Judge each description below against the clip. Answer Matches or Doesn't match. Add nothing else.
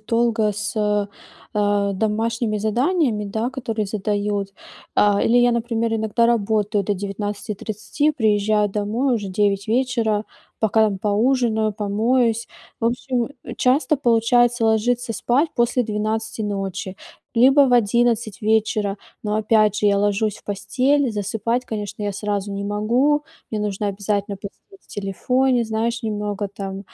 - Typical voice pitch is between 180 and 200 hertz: Doesn't match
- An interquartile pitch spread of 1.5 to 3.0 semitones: Matches